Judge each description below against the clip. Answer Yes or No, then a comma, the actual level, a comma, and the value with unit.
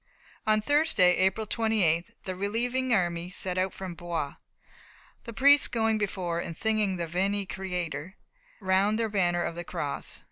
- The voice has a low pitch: No, high, 190 Hz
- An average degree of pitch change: Yes, average, 3.8 semitones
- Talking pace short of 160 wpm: Yes, average, 150 wpm